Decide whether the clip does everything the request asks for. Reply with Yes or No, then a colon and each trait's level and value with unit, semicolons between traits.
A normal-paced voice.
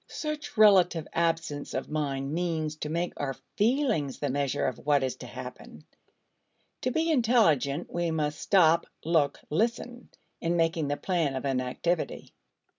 Yes: average, 150 wpm